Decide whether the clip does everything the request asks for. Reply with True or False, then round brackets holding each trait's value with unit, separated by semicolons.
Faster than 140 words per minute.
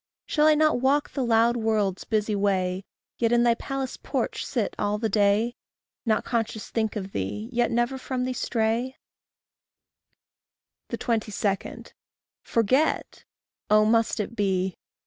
False (135 wpm)